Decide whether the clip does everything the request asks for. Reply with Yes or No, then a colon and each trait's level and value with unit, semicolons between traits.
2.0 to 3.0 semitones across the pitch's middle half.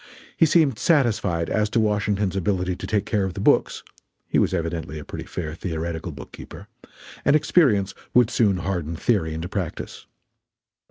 No: average, 4.5 semitones